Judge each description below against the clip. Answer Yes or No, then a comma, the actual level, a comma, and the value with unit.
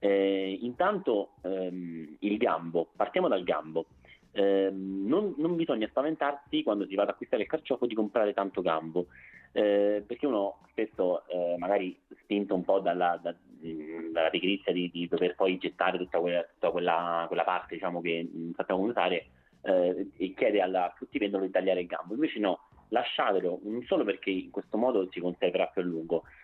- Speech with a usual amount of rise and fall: Yes, average, 3.1 semitones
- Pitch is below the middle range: Yes, very low, 95 Hz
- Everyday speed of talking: No, fast, 175 wpm